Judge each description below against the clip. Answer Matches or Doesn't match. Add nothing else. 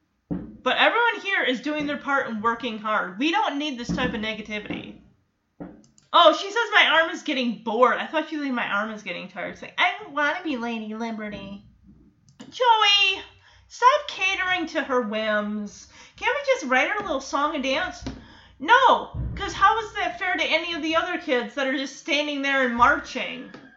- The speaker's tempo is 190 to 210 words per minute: Matches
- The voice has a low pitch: Doesn't match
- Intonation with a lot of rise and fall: Matches